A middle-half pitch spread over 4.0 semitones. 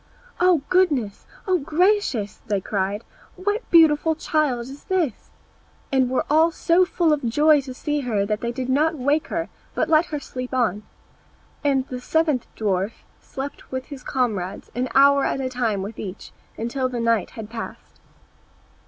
Yes: average, 4.9 semitones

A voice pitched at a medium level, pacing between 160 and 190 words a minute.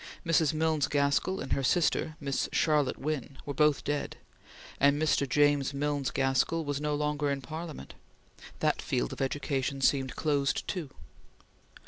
No: medium, 145 Hz; average, 145 wpm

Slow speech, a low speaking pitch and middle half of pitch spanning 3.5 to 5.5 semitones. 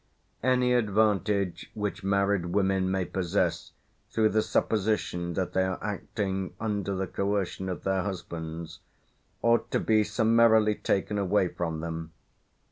No: slow, 130 wpm; low, 100 Hz; narrow, 2.6 semitones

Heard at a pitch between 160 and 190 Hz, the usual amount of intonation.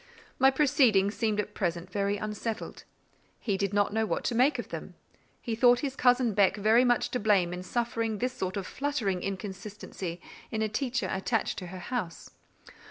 No: high, 215 Hz; average, 4.0 semitones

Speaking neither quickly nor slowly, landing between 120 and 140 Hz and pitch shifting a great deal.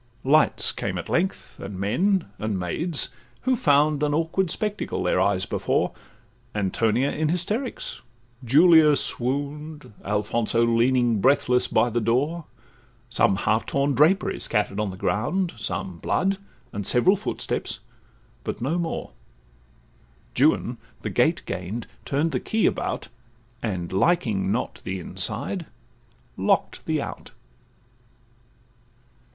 No: slow, 120 wpm; low, 135 Hz; wide, 7.6 semitones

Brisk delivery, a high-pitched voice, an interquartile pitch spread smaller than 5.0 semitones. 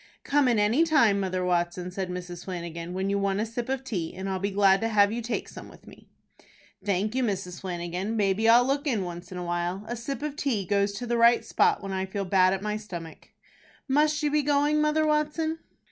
No: fast, 230 wpm; high, 205 Hz; average, 5.3 semitones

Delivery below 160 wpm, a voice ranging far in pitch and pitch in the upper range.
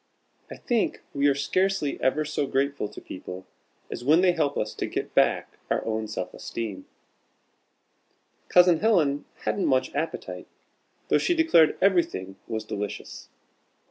No: average, 140 wpm; wide, 8.1 semitones; medium, 140 Hz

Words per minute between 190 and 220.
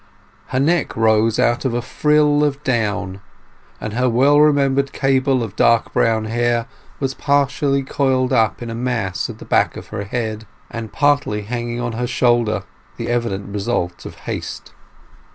No: average, 160 wpm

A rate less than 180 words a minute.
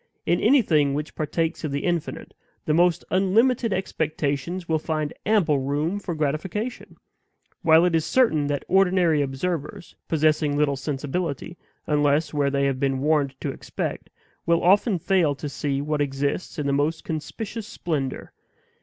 Yes: average, 150 wpm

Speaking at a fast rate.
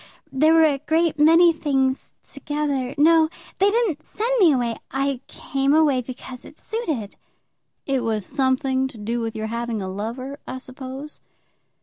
No: average, 155 wpm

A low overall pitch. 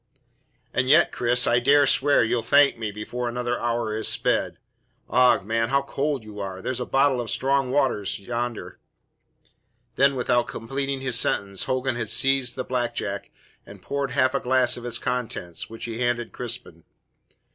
Yes: low, 125 Hz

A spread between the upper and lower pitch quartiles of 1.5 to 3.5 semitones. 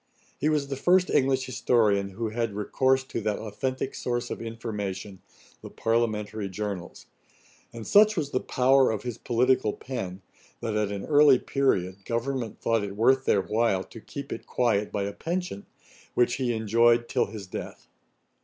No: average, 4.2 semitones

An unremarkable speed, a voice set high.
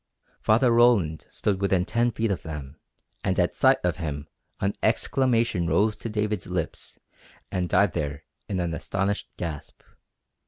No: average, 150 wpm; very low, 95 Hz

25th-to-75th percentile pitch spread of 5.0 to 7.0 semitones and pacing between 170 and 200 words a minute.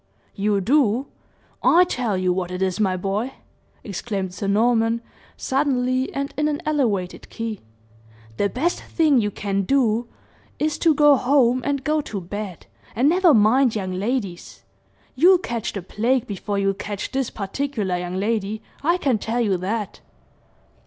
No: wide, 5.6 semitones; average, 155 wpm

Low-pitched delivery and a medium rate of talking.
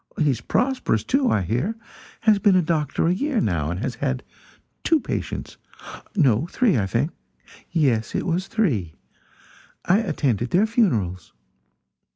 No: medium, 155 Hz; average, 150 wpm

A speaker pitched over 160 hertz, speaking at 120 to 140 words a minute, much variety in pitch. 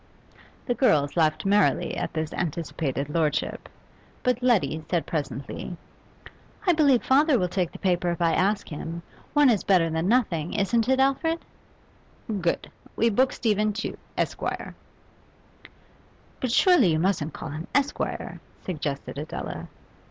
Yes: medium, 185 Hz; slow, 135 wpm; wide, 7.4 semitones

